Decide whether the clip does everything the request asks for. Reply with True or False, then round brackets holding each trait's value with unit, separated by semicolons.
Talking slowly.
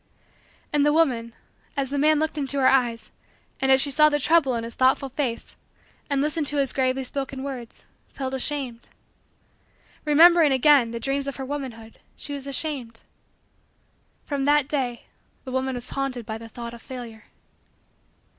False (165 wpm)